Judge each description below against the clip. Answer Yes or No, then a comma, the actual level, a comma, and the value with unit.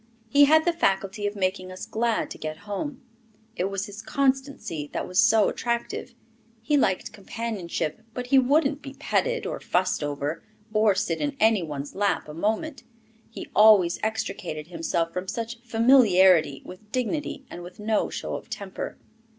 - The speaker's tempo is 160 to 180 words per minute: Yes, average, 165 wpm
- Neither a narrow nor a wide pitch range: No, wide, 5.7 semitones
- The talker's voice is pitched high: Yes, high, 215 Hz